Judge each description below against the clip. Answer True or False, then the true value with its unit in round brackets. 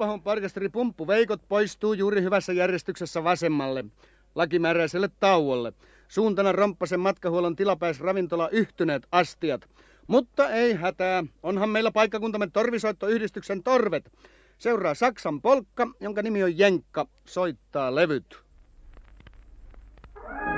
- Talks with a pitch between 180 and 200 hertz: True (190 Hz)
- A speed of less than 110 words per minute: True (95 wpm)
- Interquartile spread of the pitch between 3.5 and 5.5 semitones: True (3.9 semitones)